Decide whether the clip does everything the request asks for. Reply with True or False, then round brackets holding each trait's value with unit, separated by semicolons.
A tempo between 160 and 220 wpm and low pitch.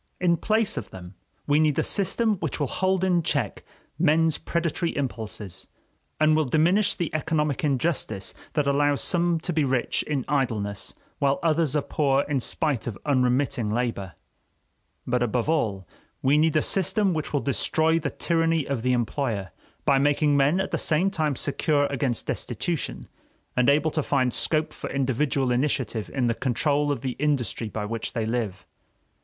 False (170 wpm; 145 Hz)